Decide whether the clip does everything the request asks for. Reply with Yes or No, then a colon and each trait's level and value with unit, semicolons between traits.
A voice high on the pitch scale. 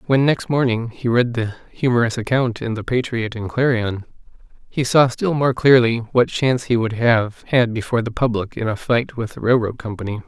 No: low, 120 Hz